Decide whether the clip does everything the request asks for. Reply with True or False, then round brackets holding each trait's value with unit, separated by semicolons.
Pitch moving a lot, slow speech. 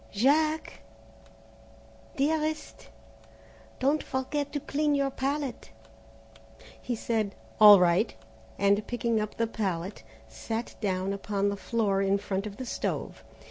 True (5.7 semitones; 120 wpm)